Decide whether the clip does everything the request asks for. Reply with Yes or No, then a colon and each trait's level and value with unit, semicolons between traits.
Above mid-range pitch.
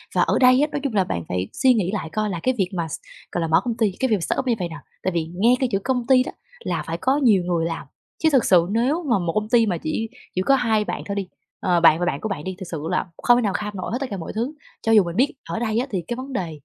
Yes: high, 210 Hz